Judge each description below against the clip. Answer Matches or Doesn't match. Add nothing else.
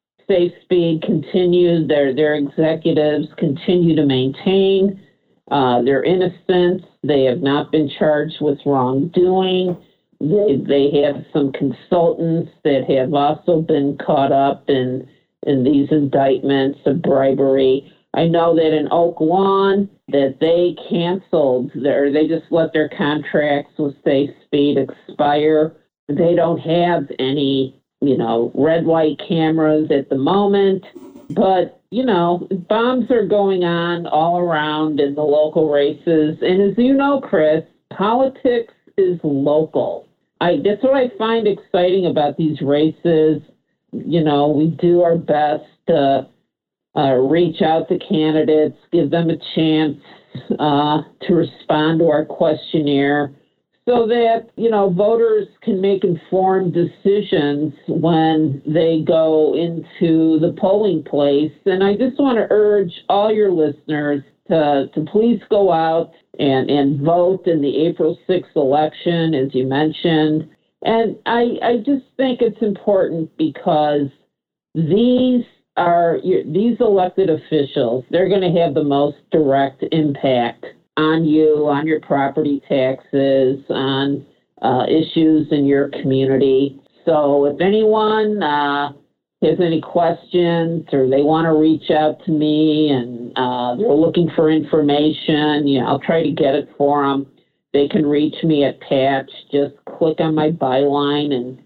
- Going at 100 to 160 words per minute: Matches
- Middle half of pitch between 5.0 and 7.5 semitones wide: Doesn't match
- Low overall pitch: Doesn't match